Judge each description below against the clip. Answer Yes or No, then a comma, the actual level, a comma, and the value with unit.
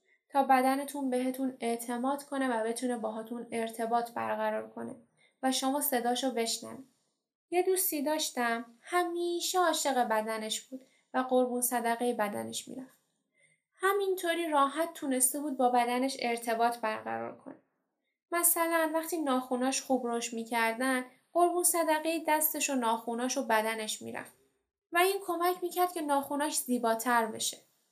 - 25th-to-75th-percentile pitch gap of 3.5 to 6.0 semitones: Yes, average, 4.9 semitones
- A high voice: Yes, very high, 260 Hz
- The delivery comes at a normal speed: Yes, average, 125 wpm